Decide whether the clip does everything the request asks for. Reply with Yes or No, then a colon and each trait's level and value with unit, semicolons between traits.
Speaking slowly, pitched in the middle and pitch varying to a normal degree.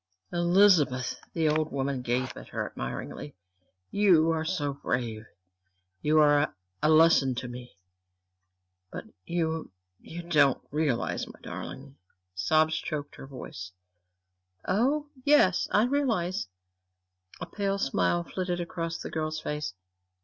Yes: slow, 130 wpm; medium, 155 Hz; average, 4.9 semitones